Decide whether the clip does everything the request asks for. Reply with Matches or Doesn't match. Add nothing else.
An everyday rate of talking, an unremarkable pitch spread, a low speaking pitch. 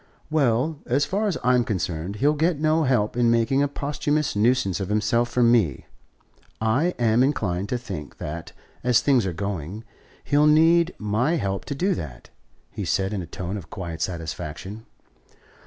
Doesn't match